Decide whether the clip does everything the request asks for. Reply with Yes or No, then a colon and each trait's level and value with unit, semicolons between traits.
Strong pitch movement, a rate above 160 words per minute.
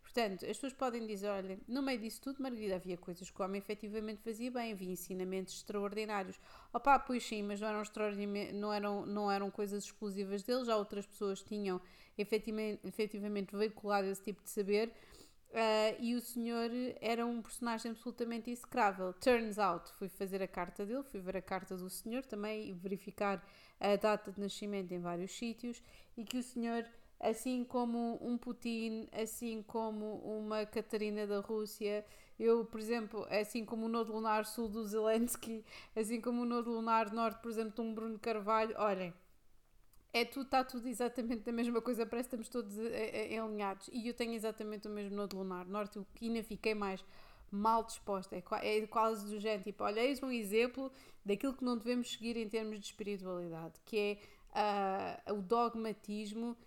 No: narrow, 2.4 semitones; average, 180 wpm